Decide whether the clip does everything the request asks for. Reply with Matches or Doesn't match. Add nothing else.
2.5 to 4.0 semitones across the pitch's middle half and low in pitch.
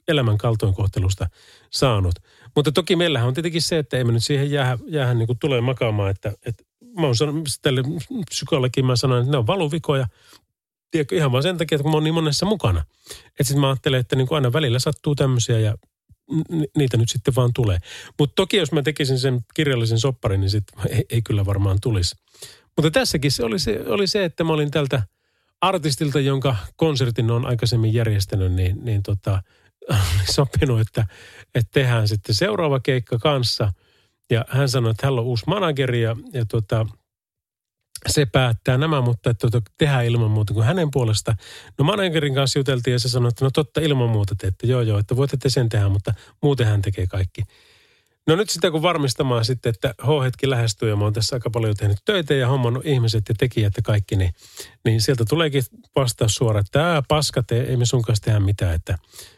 Doesn't match